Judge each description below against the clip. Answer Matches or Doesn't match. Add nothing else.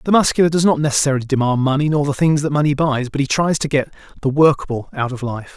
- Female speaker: Doesn't match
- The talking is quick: Matches